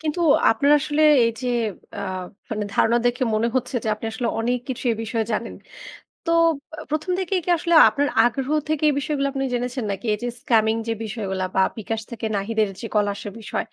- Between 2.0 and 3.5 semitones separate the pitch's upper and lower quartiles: No, average, 4.2 semitones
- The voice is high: Yes, high, 240 Hz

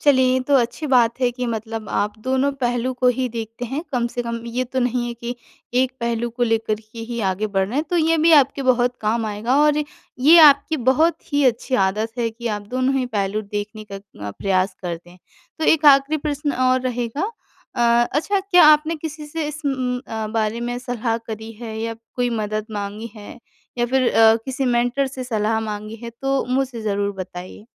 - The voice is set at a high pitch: Yes, high, 245 Hz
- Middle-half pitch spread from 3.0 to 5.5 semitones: Yes, average, 3.4 semitones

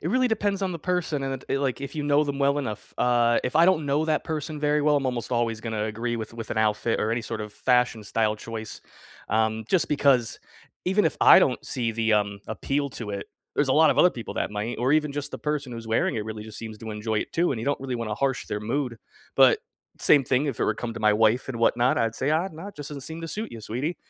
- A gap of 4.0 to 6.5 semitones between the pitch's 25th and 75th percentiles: Yes, average, 4.9 semitones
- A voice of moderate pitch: No, low, 125 Hz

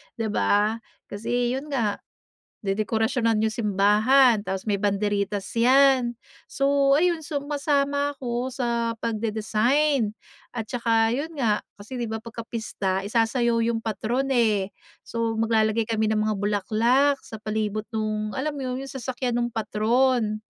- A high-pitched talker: Yes, high, 230 Hz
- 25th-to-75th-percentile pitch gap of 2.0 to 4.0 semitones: Yes, average, 3.3 semitones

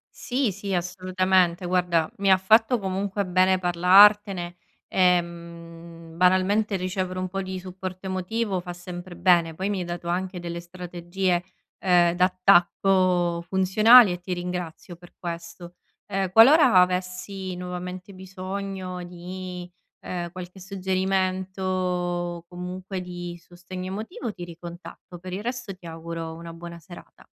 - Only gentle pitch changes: Yes, narrow, 1.4 semitones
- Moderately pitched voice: Yes, medium, 180 Hz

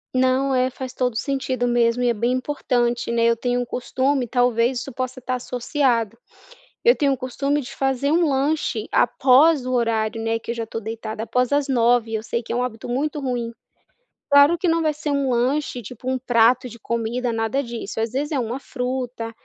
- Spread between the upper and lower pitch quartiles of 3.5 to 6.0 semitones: No, narrow, 2.6 semitones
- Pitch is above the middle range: Yes, very high, 250 Hz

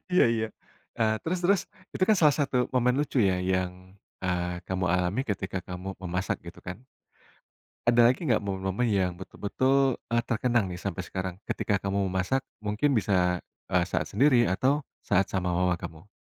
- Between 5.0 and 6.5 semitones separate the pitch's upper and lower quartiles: Yes, average, 5.3 semitones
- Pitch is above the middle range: No, low, 100 Hz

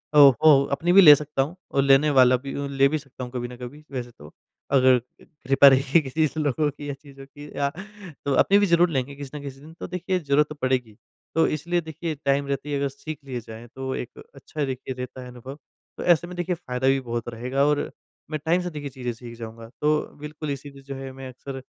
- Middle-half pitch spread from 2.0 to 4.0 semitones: Yes, average, 2.7 semitones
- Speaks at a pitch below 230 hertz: Yes, medium, 140 Hz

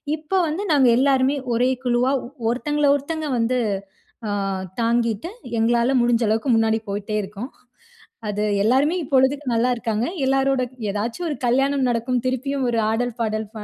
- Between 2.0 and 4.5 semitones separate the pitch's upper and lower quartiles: Yes, average, 3.1 semitones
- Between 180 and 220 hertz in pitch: No, very high, 250 Hz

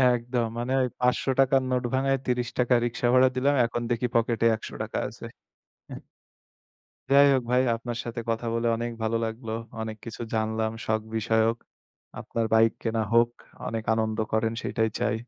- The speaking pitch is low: Yes, low, 115 Hz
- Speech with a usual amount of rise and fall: No, narrow, 1.8 semitones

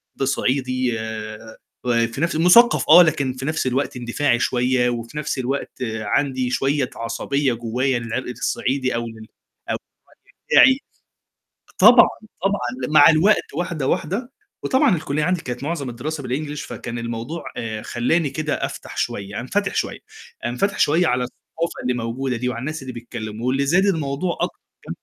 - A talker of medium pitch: No, low, 130 Hz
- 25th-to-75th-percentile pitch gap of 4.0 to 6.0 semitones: Yes, average, 4.4 semitones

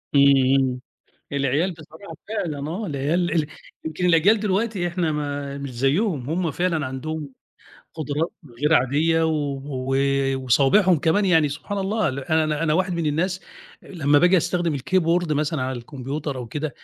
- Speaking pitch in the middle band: Yes, medium, 155 Hz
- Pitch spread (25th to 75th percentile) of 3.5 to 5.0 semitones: Yes, average, 3.9 semitones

